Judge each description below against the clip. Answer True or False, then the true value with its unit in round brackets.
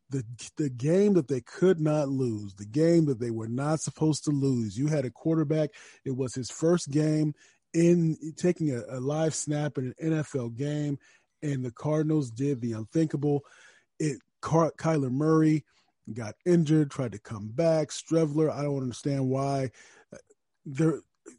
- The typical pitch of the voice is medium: True (145 Hz)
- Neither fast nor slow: True (160 wpm)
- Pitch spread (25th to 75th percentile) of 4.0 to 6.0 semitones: False (3.1 semitones)